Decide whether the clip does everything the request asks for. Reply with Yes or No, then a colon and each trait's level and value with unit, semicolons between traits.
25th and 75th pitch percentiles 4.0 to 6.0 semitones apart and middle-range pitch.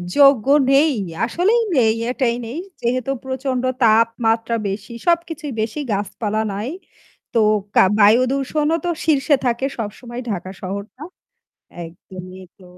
No: average, 4.3 semitones; high, 235 Hz